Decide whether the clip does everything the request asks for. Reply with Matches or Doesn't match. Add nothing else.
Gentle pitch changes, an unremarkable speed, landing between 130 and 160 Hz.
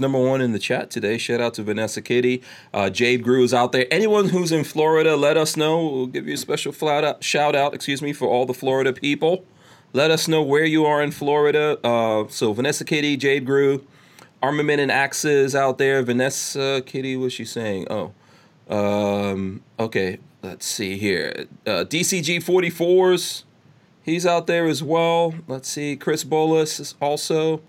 Doesn't match